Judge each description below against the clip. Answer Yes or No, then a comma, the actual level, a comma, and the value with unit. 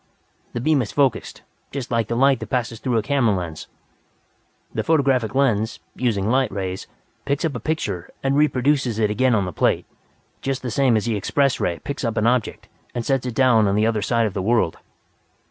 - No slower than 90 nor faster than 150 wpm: No, fast, 205 wpm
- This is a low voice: Yes, low, 120 Hz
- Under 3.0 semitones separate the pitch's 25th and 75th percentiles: No, average, 4.1 semitones